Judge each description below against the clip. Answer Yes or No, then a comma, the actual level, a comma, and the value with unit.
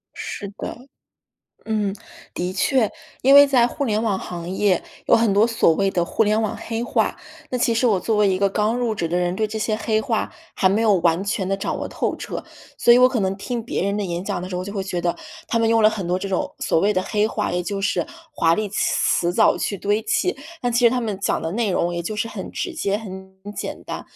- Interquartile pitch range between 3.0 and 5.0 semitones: Yes, average, 3.3 semitones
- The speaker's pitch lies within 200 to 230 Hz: Yes, high, 210 Hz